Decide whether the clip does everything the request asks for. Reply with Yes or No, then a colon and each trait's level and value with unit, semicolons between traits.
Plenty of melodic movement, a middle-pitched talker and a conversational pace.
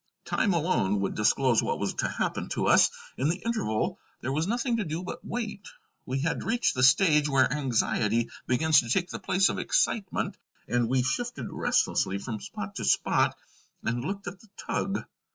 Yes: wide, 8.2 semitones; medium, 150 Hz; average, 185 wpm